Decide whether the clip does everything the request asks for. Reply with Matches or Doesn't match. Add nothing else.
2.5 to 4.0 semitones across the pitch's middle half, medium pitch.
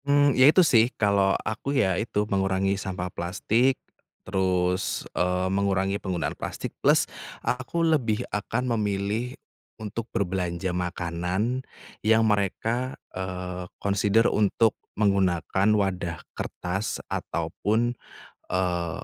Doesn't match